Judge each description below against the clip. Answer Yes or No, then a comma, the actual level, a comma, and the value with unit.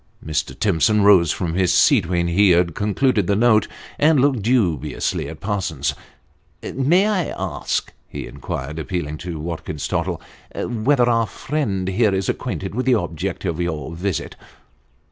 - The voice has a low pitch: Yes, very low, 95 Hz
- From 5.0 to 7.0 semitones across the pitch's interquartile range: Yes, wide, 5.6 semitones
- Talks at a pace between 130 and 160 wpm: Yes, average, 155 wpm